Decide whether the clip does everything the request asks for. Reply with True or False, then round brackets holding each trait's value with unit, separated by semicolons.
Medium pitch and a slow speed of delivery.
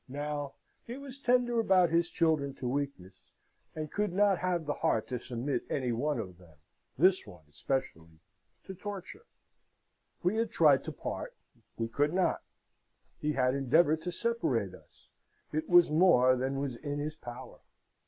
False (145 Hz; 160 wpm)